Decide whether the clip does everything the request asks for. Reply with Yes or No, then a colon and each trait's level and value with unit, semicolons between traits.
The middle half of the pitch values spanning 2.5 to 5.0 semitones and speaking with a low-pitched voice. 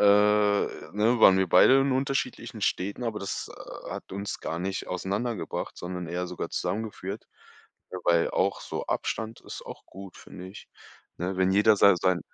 Yes: average, 2.8 semitones; low, 100 Hz